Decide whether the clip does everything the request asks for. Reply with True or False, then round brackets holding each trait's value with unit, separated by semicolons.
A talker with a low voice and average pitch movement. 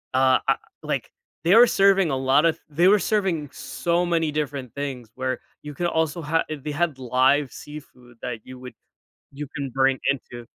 False (145 Hz; 4.5 semitones)